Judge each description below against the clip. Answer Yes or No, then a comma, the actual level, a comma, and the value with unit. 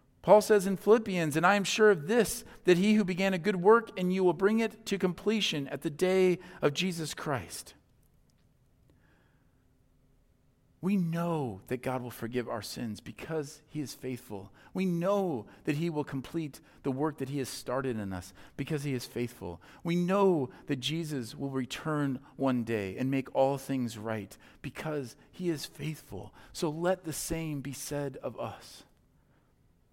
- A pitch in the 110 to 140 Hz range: No, medium, 150 Hz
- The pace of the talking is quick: No, average, 170 wpm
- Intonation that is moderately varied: No, wide, 5.9 semitones